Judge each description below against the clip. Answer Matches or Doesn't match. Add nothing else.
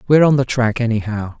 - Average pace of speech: Doesn't match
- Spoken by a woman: Doesn't match